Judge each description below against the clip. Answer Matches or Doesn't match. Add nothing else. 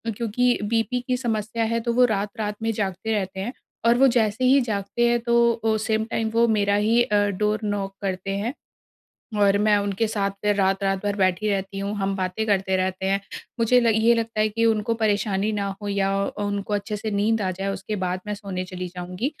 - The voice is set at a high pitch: Matches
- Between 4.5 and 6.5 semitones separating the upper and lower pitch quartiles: Doesn't match